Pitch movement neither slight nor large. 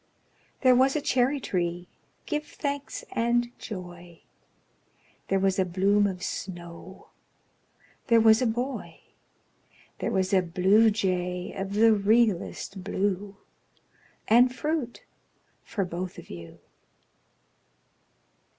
Yes: average, 4.7 semitones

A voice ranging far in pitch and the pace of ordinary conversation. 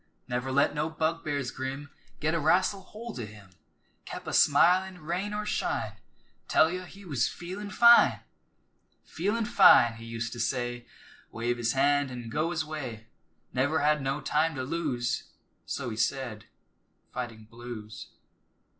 Yes: wide, 5.7 semitones; average, 150 wpm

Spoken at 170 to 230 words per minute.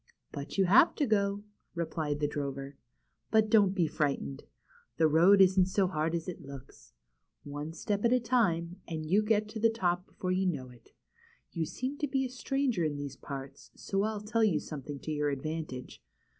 Yes: average, 190 wpm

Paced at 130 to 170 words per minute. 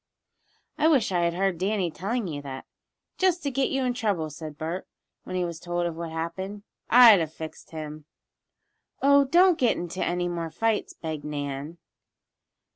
No: average, 180 wpm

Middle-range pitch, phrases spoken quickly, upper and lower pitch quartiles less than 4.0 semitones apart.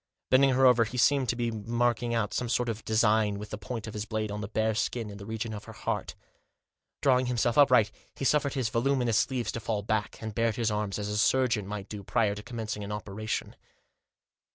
No: low, 110 Hz; fast, 225 wpm; narrow, 2.6 semitones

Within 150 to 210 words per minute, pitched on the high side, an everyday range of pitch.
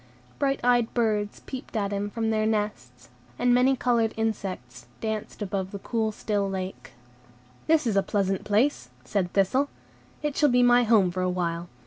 Yes: average, 170 wpm; high, 210 Hz; average, 4.0 semitones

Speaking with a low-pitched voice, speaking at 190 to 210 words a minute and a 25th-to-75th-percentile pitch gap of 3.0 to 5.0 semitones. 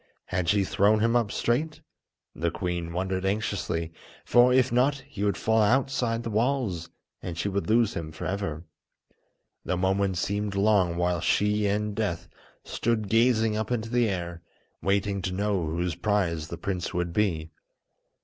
No: low, 100 Hz; average, 160 wpm; average, 4.0 semitones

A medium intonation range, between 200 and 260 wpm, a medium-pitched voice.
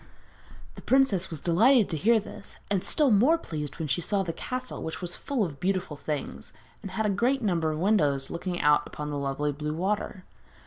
No: wide, 6.1 semitones; fast, 205 wpm; medium, 180 Hz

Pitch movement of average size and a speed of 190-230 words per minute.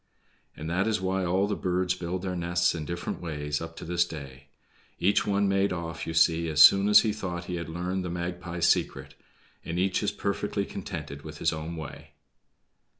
No: narrow, 2.2 semitones; average, 200 wpm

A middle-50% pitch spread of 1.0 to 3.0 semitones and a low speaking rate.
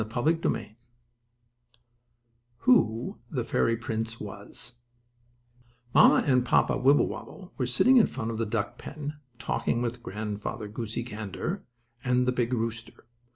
Yes: narrow, 2.4 semitones; slow, 125 wpm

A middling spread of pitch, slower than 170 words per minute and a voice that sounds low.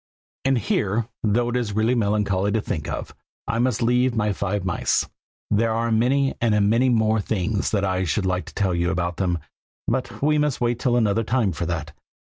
No: average, 3.8 semitones; fast, 205 wpm; low, 110 Hz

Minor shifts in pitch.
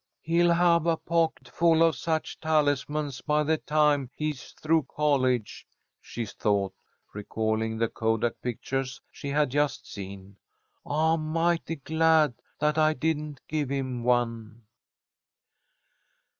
No: average, 4.7 semitones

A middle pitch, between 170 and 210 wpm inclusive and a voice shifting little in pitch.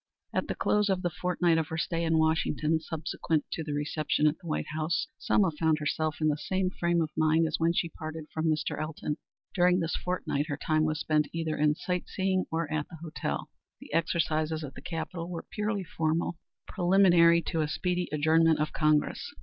Yes: medium, 160 Hz; average, 200 wpm; narrow, 1.9 semitones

